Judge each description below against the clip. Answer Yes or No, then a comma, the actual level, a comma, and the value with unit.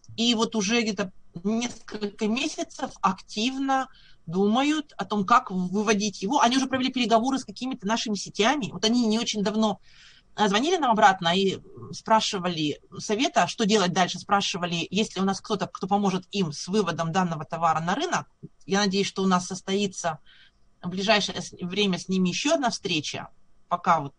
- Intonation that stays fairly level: No, average, 3.8 semitones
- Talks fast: Yes, fast, 165 wpm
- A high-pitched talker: Yes, high, 200 Hz